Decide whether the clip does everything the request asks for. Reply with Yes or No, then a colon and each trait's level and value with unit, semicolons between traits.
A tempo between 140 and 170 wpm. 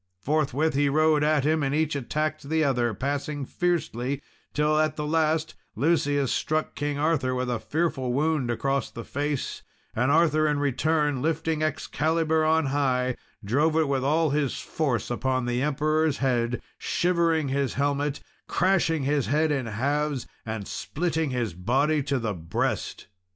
Yes: average, 155 wpm